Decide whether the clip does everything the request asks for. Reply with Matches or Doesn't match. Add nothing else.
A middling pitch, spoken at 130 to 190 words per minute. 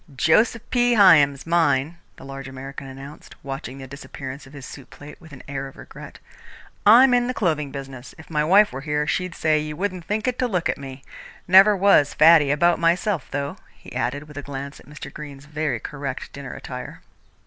Doesn't match